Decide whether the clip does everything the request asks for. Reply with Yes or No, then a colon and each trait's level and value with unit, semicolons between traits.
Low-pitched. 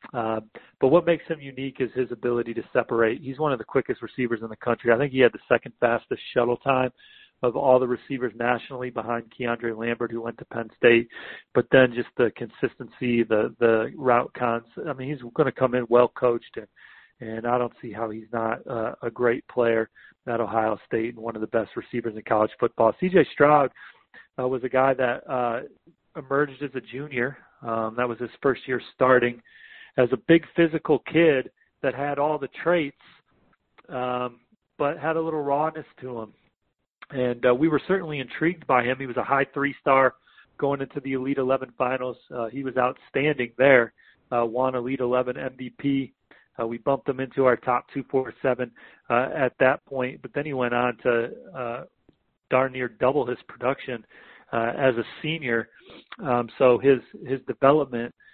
Yes: low, 125 Hz